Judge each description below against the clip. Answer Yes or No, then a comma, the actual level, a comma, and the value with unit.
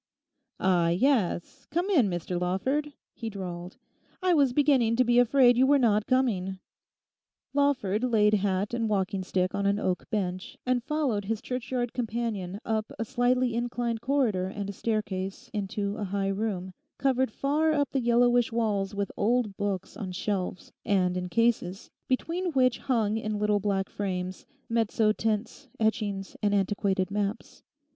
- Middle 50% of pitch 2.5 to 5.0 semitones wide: Yes, average, 4.0 semitones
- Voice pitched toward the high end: Yes, high, 215 Hz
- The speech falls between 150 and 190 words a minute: Yes, average, 155 wpm